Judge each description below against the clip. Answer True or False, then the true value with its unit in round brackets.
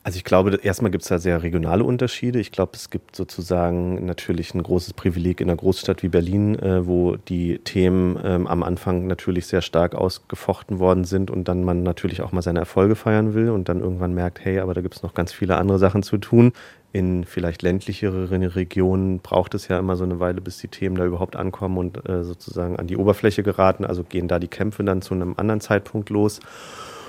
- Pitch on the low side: True (95 Hz)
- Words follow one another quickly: True (210 wpm)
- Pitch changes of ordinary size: False (1.8 semitones)